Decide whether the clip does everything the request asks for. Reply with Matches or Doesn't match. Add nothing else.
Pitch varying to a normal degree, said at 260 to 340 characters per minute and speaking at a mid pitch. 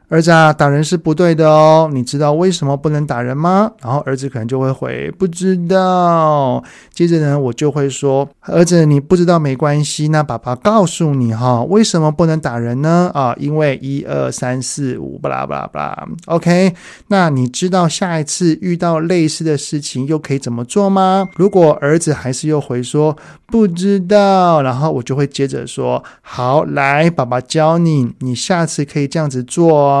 Matches